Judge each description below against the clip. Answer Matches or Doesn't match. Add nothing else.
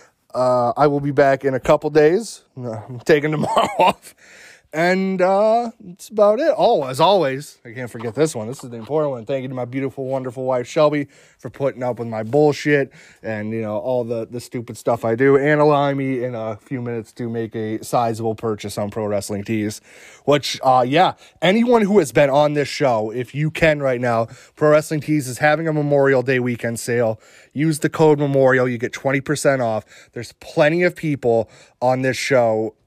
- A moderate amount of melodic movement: Matches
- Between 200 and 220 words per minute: Matches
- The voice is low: Matches